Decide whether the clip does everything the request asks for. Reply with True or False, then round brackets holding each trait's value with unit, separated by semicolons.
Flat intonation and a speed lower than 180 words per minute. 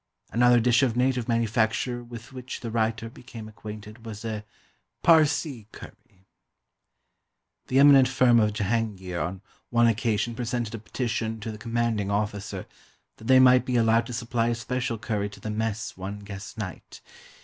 True (2.3 semitones; 160 wpm)